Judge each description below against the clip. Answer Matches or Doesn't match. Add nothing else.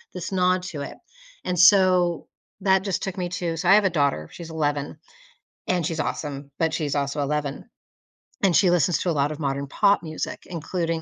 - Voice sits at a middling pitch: Matches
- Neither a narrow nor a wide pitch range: Matches